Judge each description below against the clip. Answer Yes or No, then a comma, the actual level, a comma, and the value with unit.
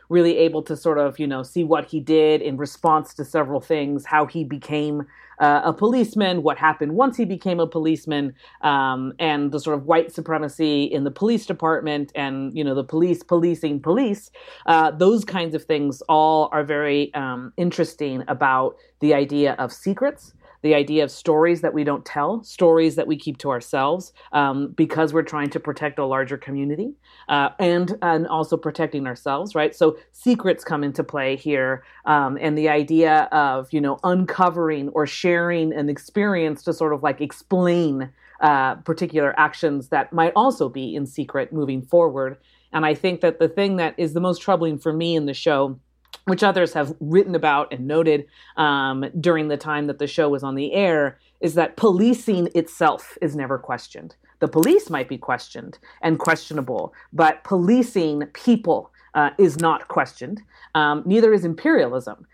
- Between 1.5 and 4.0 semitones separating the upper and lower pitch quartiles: Yes, average, 2.9 semitones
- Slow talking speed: No, average, 180 wpm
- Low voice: No, medium, 155 Hz